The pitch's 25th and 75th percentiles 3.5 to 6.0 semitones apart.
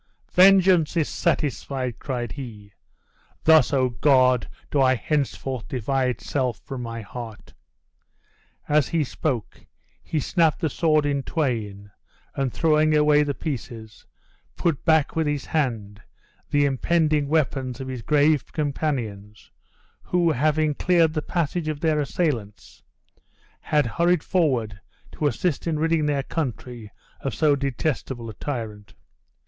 Yes: average, 4.1 semitones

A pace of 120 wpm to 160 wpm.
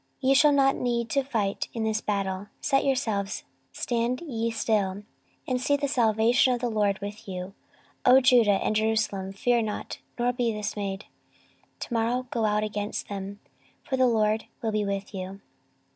No: average, 175 wpm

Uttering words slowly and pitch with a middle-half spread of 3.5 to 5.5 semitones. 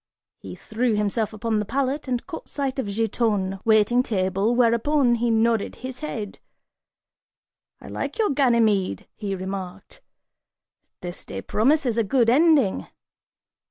Yes: slow, 130 wpm; average, 4.1 semitones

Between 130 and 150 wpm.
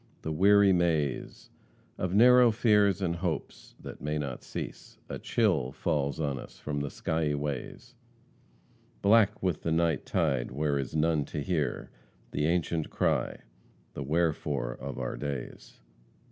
Yes: average, 145 wpm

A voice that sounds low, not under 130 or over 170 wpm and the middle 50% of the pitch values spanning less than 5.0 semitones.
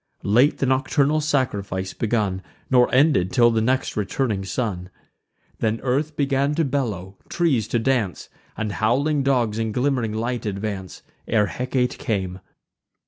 Yes: low, 120 Hz; average, 140 wpm; average, 4.5 semitones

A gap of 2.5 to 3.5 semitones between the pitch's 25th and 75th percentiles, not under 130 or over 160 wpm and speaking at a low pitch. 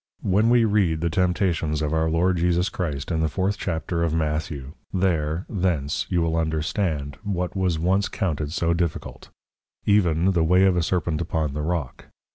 No: average, 2.8 semitones; average, 175 wpm; very low, 85 Hz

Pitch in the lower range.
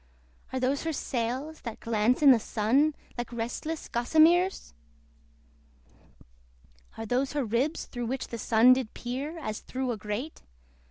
No: very high, 255 Hz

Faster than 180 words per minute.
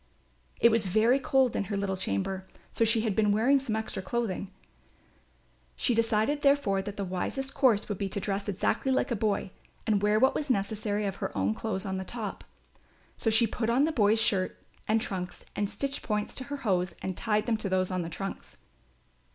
Yes: fast, 205 wpm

